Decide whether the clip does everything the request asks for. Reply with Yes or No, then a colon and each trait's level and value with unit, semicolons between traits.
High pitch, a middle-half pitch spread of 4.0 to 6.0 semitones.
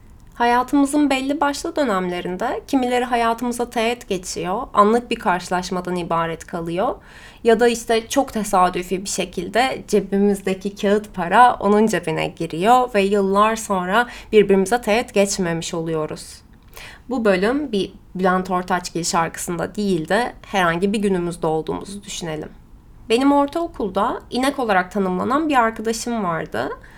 Yes: high, 205 Hz; average, 4.7 semitones